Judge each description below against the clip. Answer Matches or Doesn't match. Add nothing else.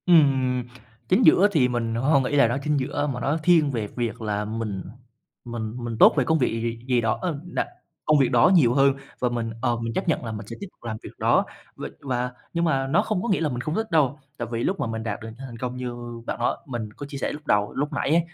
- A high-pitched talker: Doesn't match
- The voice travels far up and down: Doesn't match